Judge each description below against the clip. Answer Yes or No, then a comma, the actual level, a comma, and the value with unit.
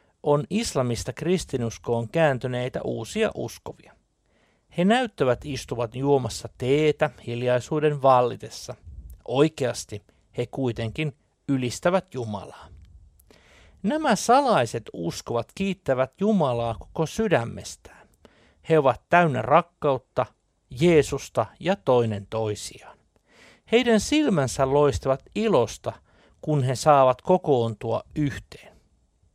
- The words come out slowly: Yes, slow, 85 wpm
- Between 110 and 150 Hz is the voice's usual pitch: Yes, low, 130 Hz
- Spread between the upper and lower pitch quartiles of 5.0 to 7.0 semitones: Yes, average, 5.3 semitones